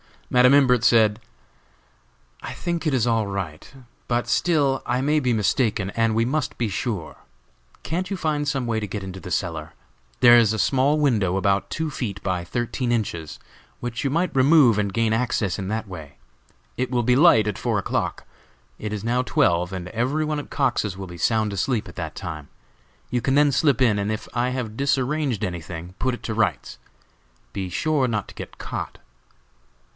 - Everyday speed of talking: Yes, average, 190 wpm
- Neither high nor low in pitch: No, low, 115 Hz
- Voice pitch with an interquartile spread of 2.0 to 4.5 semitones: No, average, 5.1 semitones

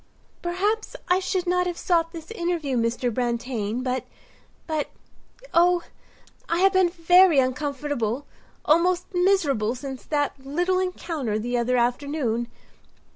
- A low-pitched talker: No, very high, 300 Hz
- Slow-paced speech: Yes, slow, 120 wpm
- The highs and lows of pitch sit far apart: Yes, wide, 6.1 semitones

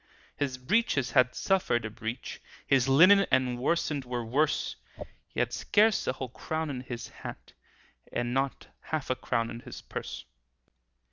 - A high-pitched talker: No, low, 130 Hz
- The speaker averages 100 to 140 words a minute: No, average, 155 wpm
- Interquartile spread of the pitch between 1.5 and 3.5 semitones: No, average, 4.1 semitones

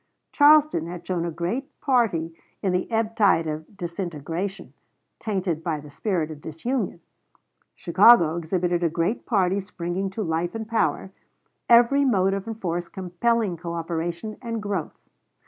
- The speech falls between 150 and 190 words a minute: No, slow, 135 wpm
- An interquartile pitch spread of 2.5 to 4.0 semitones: No, average, 4.8 semitones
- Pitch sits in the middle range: Yes, medium, 180 Hz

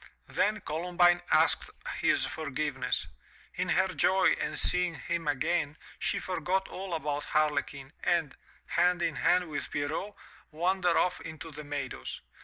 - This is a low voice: No, medium, 170 Hz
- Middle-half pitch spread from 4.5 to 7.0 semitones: No, average, 3.0 semitones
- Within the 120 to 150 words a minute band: Yes, slow, 135 wpm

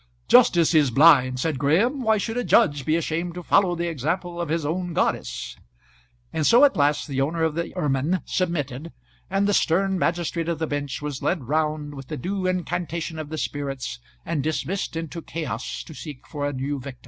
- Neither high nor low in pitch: Yes, medium, 160 Hz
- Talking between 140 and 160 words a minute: No, average, 195 wpm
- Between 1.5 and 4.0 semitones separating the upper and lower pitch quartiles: Yes, average, 3.4 semitones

